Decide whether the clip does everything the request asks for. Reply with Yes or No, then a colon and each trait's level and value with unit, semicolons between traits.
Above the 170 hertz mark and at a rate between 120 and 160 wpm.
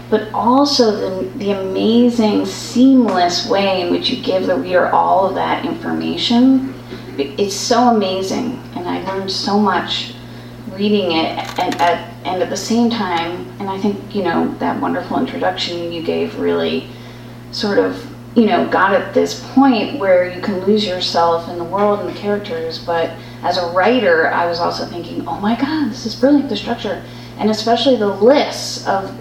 No: medium, 185 Hz; average, 180 wpm